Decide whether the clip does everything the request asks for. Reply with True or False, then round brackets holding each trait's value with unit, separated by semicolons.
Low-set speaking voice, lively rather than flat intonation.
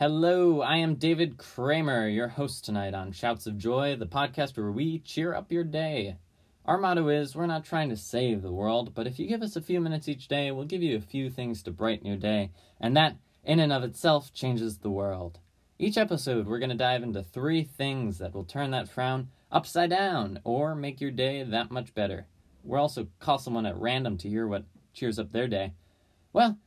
True (125 Hz; 6.3 semitones)